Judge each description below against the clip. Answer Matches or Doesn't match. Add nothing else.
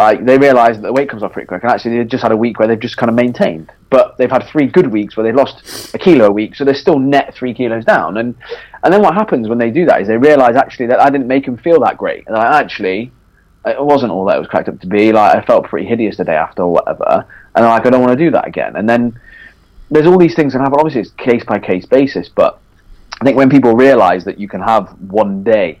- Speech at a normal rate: Doesn't match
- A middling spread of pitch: Matches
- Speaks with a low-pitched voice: Matches